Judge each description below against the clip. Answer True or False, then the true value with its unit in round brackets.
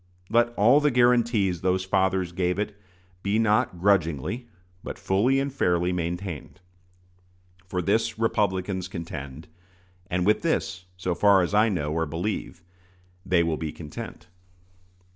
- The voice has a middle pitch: False (95 Hz)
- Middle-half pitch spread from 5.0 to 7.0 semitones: False (3.6 semitones)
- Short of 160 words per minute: True (135 wpm)